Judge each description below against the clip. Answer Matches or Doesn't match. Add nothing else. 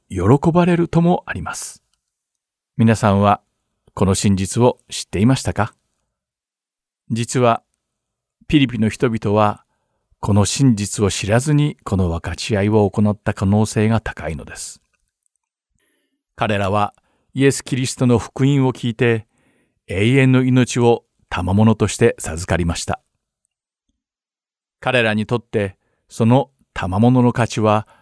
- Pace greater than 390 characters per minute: Doesn't match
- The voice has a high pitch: Doesn't match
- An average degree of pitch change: Matches